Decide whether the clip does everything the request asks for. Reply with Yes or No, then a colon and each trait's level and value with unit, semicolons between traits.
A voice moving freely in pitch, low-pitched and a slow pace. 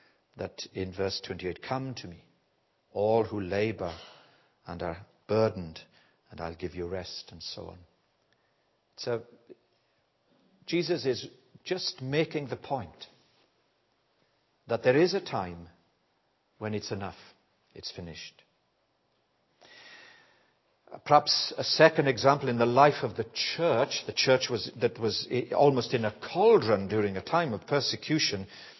Yes: wide, 6.9 semitones; low, 115 Hz; slow, 130 wpm